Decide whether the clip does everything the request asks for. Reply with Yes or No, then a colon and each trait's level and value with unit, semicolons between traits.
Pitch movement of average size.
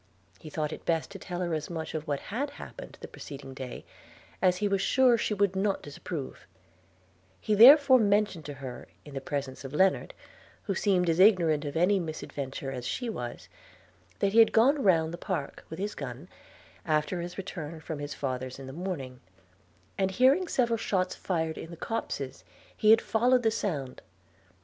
No: wide, 6.0 semitones